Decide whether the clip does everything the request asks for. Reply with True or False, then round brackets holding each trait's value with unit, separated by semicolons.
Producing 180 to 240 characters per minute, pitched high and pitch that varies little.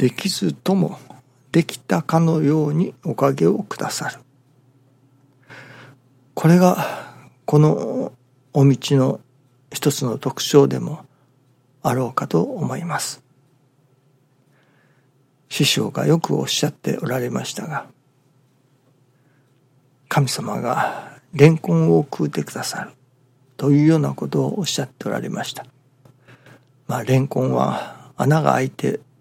False (225 characters per minute; 135 Hz; 1.7 semitones)